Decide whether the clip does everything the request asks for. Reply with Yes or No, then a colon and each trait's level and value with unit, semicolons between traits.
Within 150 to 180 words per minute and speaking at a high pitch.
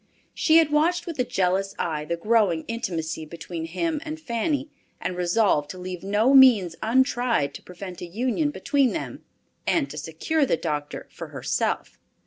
Yes: average, 165 wpm; high, 200 Hz